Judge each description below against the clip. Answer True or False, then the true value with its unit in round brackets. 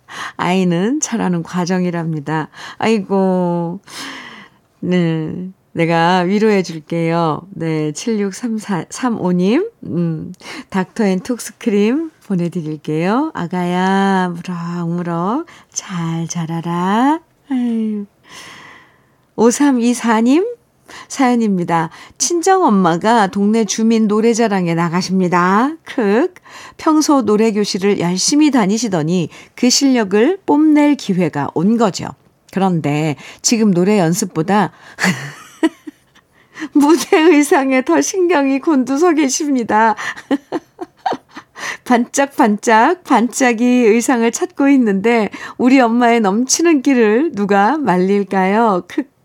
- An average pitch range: False (6.7 semitones)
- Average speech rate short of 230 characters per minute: True (205 characters per minute)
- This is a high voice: True (215 Hz)